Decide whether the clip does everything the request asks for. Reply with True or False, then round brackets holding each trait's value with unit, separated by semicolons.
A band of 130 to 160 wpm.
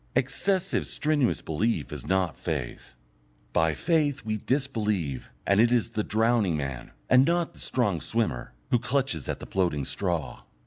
True (150 wpm)